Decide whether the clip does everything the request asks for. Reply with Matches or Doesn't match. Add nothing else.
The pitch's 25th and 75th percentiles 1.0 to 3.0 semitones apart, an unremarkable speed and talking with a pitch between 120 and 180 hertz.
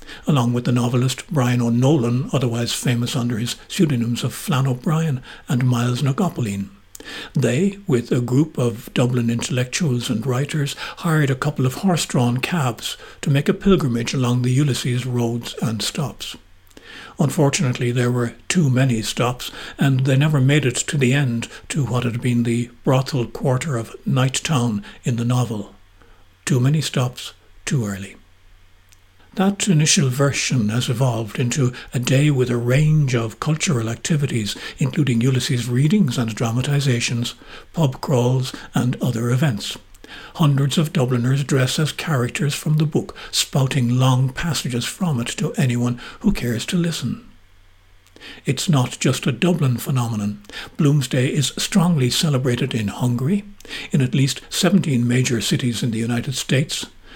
Doesn't match